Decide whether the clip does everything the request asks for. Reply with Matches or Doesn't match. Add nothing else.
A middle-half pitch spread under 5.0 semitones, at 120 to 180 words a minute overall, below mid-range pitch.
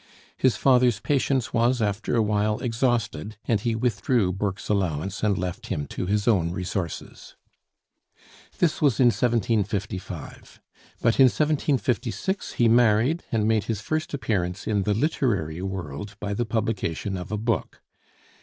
Matches